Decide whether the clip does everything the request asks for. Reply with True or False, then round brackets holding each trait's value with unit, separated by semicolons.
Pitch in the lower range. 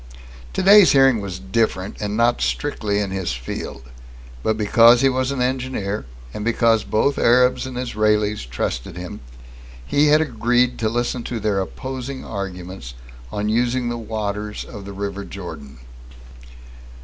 True (110 Hz)